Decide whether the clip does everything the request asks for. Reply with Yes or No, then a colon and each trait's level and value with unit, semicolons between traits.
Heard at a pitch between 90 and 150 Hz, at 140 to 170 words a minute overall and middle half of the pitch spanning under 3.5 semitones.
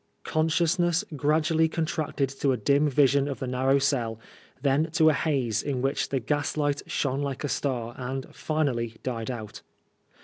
Yes: medium, 140 Hz; average, 160 wpm; average, 3.1 semitones